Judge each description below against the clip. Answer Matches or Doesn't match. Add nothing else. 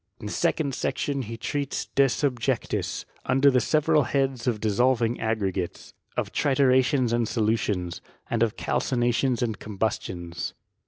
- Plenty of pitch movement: Doesn't match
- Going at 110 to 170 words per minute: Matches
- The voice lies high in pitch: Doesn't match